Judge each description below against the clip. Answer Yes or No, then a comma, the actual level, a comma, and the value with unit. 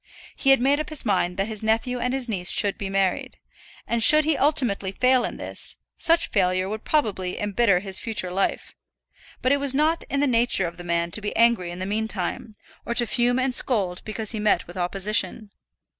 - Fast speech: Yes, fast, 210 wpm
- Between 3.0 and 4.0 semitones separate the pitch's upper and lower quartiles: No, average, 4.9 semitones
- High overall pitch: Yes, high, 220 Hz